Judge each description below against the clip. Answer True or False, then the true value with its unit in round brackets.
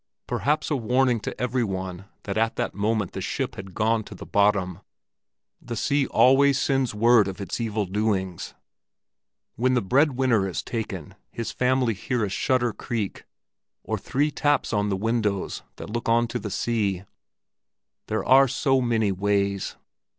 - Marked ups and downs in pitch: False (4.1 semitones)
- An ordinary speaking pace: True (160 wpm)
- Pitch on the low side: True (110 Hz)